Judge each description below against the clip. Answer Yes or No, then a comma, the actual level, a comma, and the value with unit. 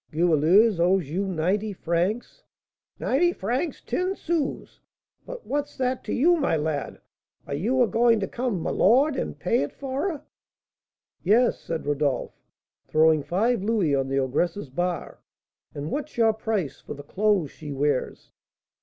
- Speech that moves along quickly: No, average, 155 wpm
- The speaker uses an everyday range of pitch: No, wide, 8.0 semitones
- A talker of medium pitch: No, high, 195 Hz